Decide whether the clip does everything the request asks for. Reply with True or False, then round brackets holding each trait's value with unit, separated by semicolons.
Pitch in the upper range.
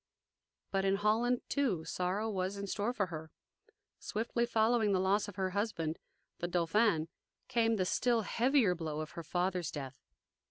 True (195 Hz)